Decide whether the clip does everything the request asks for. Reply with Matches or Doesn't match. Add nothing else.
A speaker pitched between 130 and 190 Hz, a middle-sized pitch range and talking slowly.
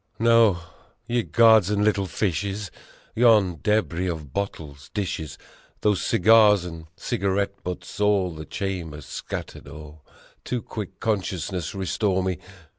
Doesn't match